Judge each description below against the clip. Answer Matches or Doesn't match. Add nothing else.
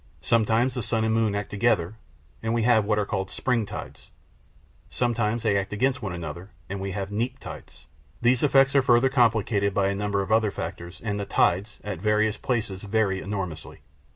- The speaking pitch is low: Matches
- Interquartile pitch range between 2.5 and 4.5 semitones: Matches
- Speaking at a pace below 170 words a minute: Doesn't match